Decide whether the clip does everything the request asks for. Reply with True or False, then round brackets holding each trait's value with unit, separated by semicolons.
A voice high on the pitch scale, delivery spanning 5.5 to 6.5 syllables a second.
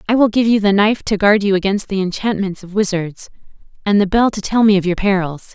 True (200 Hz; 6.0 syllables/s)